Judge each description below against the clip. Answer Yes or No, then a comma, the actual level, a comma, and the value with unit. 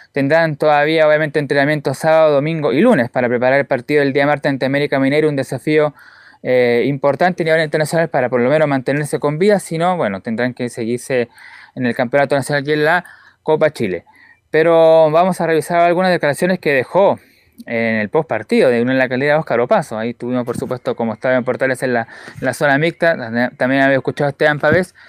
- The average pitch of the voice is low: No, medium, 145 Hz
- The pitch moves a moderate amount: Yes, average, 3.8 semitones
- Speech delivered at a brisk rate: Yes, fast, 210 wpm